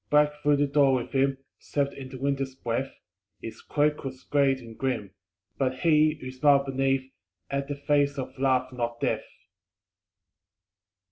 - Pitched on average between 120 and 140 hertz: Yes, low, 135 Hz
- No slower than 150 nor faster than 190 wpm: Yes, average, 160 wpm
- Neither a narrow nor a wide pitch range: No, narrow, 1.6 semitones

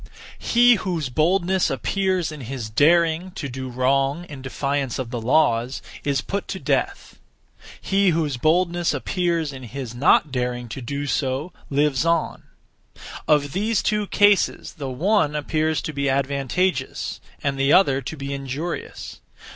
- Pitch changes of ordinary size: Yes, average, 4.4 semitones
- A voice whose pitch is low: No, medium, 145 Hz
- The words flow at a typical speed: Yes, average, 145 wpm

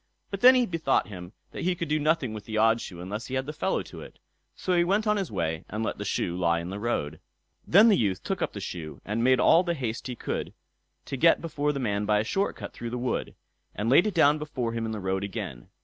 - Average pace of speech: No, fast, 270 wpm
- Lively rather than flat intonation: Yes, wide, 8.3 semitones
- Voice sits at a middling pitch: No, low, 120 Hz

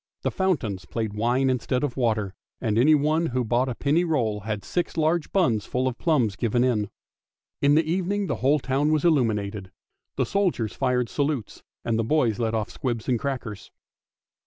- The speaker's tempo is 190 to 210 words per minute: No, average, 180 wpm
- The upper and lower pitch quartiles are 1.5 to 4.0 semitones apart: No, wide, 5.5 semitones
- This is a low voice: Yes, low, 125 Hz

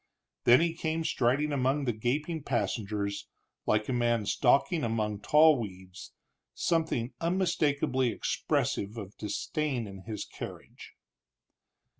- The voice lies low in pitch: Yes, low, 125 Hz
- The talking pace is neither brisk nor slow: No, slow, 115 wpm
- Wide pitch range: Yes, wide, 6.0 semitones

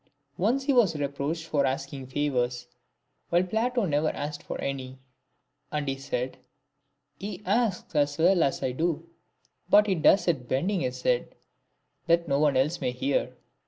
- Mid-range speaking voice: Yes, medium, 150 Hz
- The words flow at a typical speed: Yes, average, 165 wpm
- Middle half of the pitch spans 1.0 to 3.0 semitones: No, average, 4.8 semitones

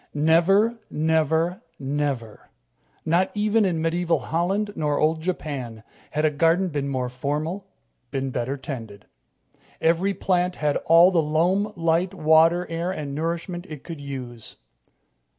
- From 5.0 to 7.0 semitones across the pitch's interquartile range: No, average, 3.8 semitones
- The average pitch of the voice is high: No, medium, 160 Hz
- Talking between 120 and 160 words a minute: Yes, slow, 135 wpm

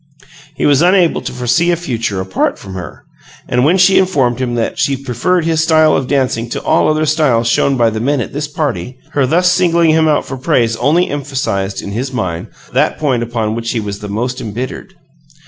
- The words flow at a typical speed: No, fast, 210 wpm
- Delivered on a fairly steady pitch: No, average, 5.2 semitones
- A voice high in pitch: No, low, 130 Hz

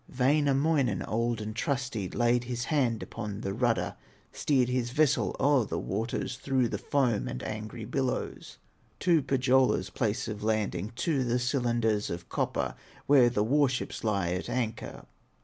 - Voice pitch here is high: No, low, 120 Hz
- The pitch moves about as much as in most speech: Yes, average, 3.5 semitones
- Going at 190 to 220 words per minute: No, average, 150 wpm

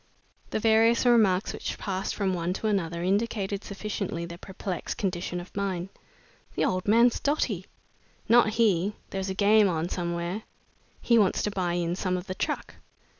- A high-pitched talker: Yes, high, 195 Hz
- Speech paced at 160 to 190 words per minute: Yes, average, 165 wpm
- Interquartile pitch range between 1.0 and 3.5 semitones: Yes, average, 3.1 semitones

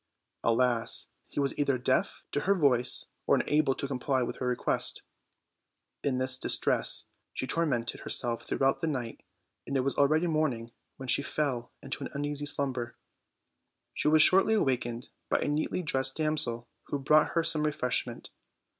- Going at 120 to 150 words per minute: No, average, 165 wpm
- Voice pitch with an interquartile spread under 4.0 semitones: Yes, average, 3.3 semitones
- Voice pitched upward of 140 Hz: No, low, 135 Hz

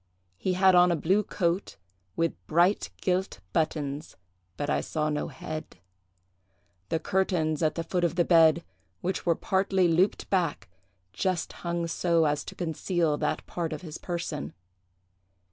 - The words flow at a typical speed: Yes, average, 150 wpm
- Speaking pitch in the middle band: Yes, medium, 170 Hz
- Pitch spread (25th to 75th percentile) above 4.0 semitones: No, narrow, 2.6 semitones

